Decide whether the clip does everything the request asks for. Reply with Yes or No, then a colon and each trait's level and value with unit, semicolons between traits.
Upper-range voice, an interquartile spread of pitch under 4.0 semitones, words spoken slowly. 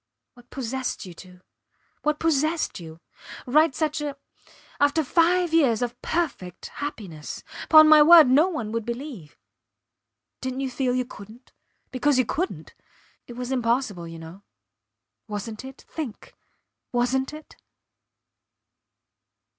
No: very high, 260 Hz; average, 5.1 semitones; slow, 125 wpm